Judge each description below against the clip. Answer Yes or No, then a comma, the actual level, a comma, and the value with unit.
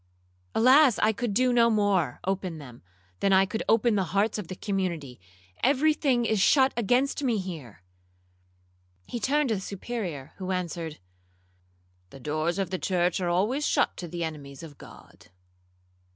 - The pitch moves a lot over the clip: Yes, wide, 6.1 semitones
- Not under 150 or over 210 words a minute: Yes, average, 155 wpm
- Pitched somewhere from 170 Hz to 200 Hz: Yes, high, 190 Hz